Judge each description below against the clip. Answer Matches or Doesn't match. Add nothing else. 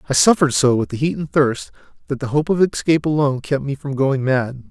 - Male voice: Matches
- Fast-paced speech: Matches